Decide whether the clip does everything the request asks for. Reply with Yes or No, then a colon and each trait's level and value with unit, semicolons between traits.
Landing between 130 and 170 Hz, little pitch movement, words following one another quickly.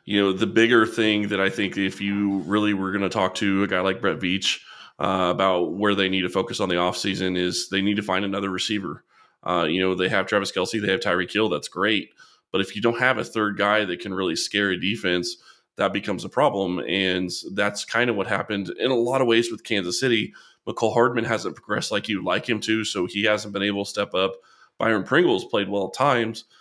No: low, 100 Hz; narrow, 2.2 semitones; fast, 240 wpm